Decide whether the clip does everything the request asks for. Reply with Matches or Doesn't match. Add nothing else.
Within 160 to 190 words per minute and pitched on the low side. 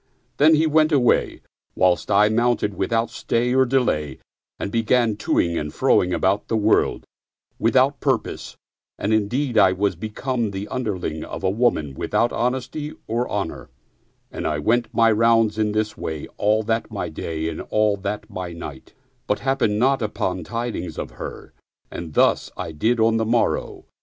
Matches